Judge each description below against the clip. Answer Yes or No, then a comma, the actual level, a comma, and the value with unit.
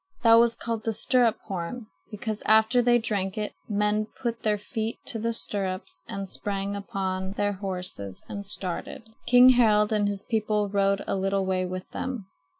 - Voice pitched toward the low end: No, high, 210 Hz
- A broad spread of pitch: No, narrow, 2.5 semitones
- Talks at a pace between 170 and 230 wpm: Yes, average, 175 wpm